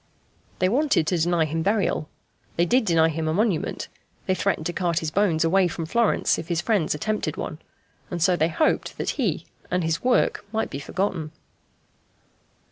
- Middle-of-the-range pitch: Yes, medium, 175 Hz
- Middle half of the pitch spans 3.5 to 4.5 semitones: Yes, average, 3.9 semitones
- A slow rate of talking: No, average, 180 wpm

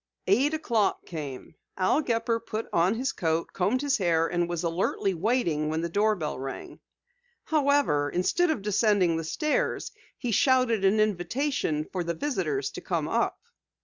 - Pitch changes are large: Yes, wide, 6.9 semitones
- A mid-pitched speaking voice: No, high, 195 Hz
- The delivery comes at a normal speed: Yes, average, 155 wpm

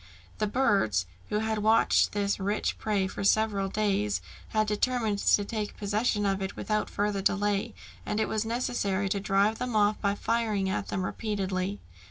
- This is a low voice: No, high, 205 Hz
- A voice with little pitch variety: Yes, narrow, 1.6 semitones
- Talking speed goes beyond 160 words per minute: Yes, average, 170 wpm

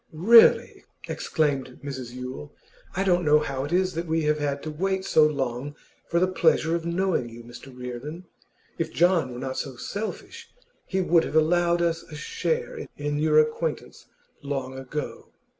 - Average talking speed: Yes, average, 170 wpm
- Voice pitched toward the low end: No, medium, 155 Hz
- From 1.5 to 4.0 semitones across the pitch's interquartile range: No, average, 4.4 semitones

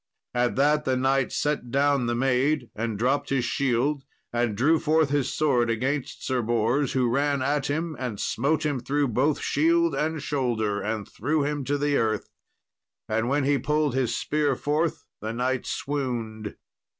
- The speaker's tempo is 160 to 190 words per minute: Yes, average, 170 wpm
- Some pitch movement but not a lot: Yes, average, 3.4 semitones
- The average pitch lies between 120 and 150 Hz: Yes, low, 135 Hz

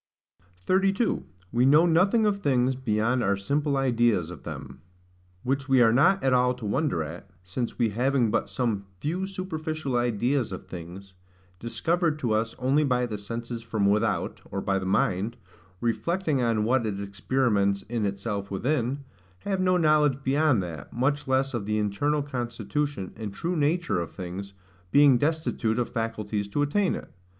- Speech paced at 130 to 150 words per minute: No, average, 165 wpm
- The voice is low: Yes, low, 120 Hz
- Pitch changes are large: Yes, wide, 5.8 semitones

